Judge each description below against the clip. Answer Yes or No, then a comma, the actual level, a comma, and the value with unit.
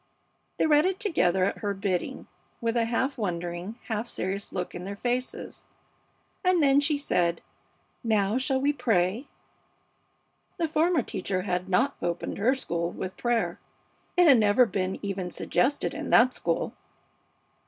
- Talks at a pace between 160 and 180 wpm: No, average, 145 wpm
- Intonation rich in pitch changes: Yes, wide, 6.8 semitones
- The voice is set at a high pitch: Yes, high, 225 Hz